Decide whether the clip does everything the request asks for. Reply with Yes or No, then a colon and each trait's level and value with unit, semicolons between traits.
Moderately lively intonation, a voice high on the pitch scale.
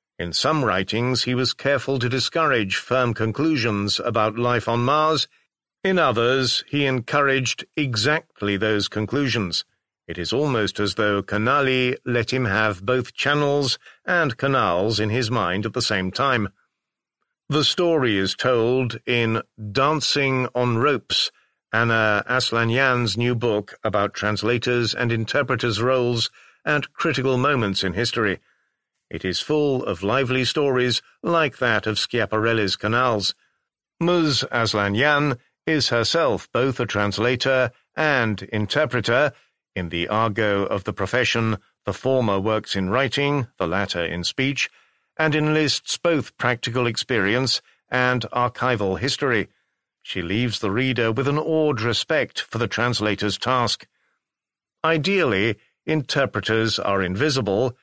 No: average, 3.9 semitones; low, 120 Hz